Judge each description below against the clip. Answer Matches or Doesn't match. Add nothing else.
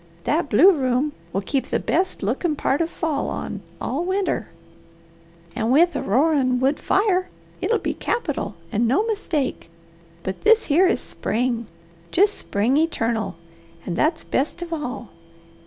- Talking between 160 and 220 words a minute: Doesn't match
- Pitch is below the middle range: Doesn't match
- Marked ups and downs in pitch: Matches